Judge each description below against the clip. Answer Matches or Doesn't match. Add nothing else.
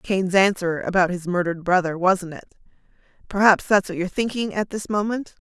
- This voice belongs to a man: Doesn't match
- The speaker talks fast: Doesn't match